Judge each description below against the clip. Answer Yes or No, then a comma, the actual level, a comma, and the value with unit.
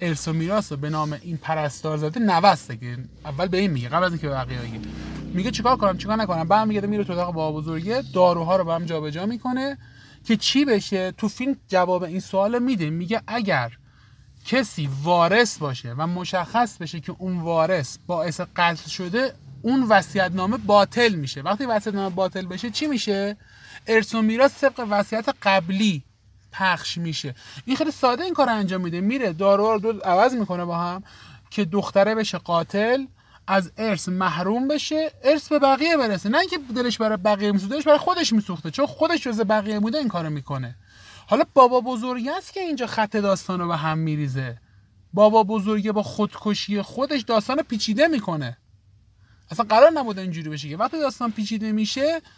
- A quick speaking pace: Yes, fast, 170 wpm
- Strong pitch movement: Yes, wide, 6.1 semitones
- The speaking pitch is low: No, high, 200 Hz